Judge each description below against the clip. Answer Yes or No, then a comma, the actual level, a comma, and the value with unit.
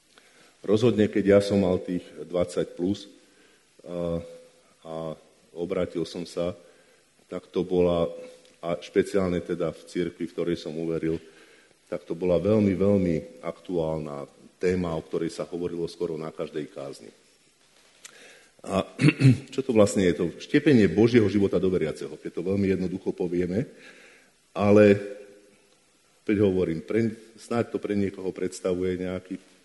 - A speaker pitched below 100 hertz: Yes, very low, 90 Hz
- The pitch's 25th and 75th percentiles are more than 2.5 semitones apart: Yes, average, 2.9 semitones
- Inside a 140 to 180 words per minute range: No, average, 130 wpm